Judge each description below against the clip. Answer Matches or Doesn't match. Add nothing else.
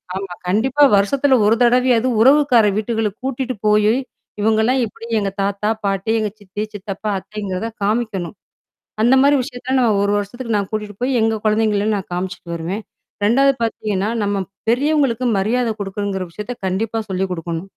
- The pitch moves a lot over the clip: Doesn't match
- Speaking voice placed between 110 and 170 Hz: Doesn't match